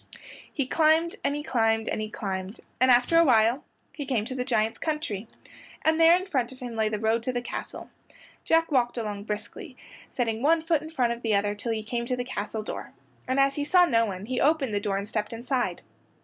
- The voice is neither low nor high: No, high, 245 Hz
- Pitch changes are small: No, average, 4.8 semitones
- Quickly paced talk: Yes, fast, 225 wpm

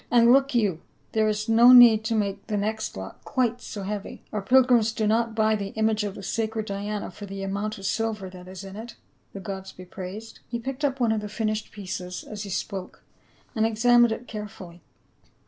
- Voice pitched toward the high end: Yes, high, 215 Hz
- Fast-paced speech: Yes, fast, 210 wpm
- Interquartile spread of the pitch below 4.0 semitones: Yes, narrow, 2.4 semitones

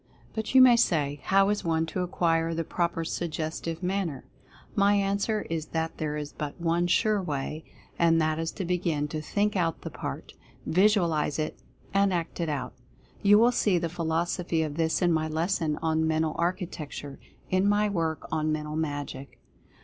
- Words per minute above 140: Yes, average, 180 wpm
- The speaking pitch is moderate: Yes, medium, 165 Hz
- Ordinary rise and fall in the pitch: Yes, average, 3.1 semitones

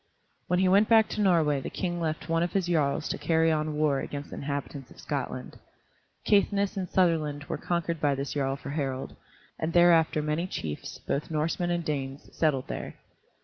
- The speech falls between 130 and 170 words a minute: No, average, 190 wpm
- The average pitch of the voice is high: No, medium, 160 Hz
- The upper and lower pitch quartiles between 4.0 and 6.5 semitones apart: No, average, 3.3 semitones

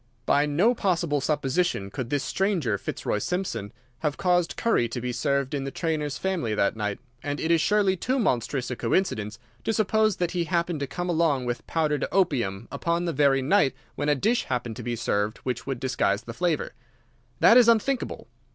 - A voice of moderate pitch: Yes, medium, 150 Hz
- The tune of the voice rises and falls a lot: Yes, wide, 6.4 semitones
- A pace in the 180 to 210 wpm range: Yes, average, 190 wpm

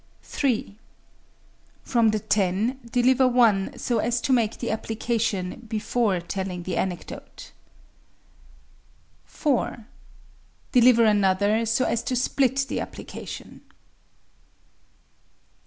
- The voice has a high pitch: Yes, high, 225 Hz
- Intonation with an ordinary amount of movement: Yes, average, 3.4 semitones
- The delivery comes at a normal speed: No, slow, 95 wpm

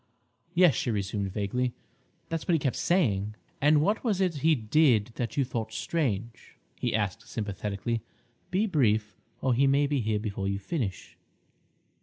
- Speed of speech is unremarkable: Yes, average, 160 wpm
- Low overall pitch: Yes, low, 120 Hz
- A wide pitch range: Yes, wide, 6.1 semitones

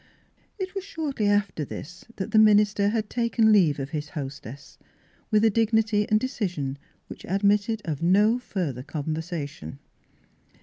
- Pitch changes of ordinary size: No, wide, 6.0 semitones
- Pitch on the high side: Yes, high, 205 Hz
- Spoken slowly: No, average, 145 wpm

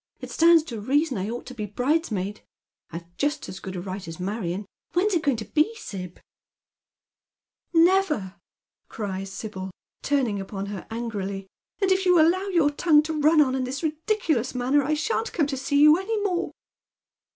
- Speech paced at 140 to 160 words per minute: No, average, 190 wpm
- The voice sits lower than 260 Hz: No, very high, 270 Hz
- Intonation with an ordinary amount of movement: No, wide, 8.2 semitones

